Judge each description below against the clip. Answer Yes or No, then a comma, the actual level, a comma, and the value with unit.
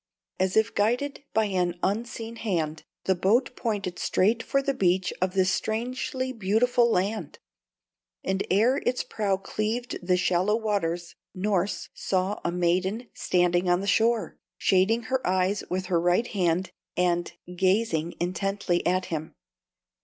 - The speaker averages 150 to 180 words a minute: No, average, 140 wpm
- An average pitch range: Yes, average, 3.8 semitones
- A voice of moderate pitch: No, high, 195 Hz